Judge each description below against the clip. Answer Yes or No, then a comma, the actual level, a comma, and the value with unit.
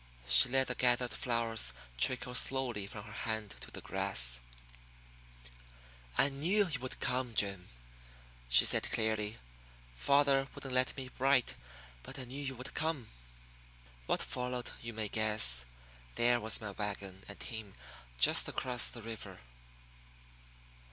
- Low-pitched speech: Yes, low, 120 Hz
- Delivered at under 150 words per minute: Yes, average, 140 wpm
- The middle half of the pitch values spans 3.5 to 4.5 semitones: Yes, average, 3.8 semitones